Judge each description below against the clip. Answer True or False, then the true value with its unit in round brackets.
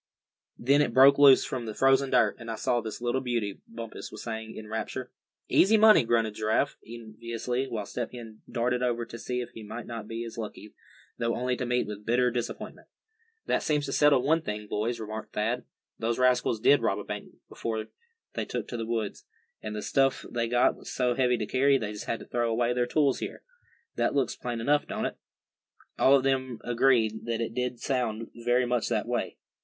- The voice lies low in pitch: True (120 Hz)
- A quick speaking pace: True (210 wpm)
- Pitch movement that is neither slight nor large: False (2.2 semitones)